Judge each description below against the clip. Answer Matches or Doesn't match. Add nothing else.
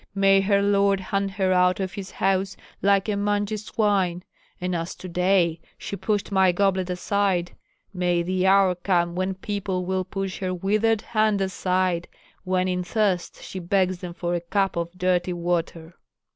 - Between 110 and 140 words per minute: Doesn't match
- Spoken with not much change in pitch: Matches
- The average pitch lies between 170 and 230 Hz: Matches